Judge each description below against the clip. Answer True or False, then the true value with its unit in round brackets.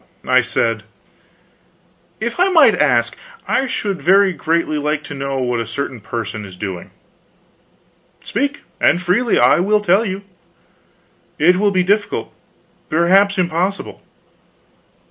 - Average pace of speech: False (125 wpm)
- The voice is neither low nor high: True (175 Hz)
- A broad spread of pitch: True (7.6 semitones)